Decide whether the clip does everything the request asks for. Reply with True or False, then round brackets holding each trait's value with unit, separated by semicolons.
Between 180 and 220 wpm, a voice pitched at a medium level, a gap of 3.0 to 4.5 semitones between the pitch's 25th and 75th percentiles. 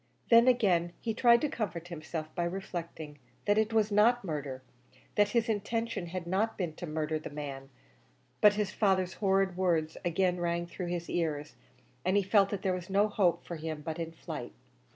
True (190 wpm; 180 Hz; 4.0 semitones)